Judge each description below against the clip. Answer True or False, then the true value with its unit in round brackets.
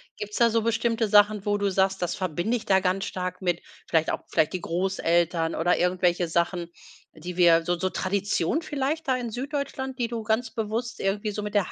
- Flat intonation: False (4.3 semitones)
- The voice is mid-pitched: False (200 Hz)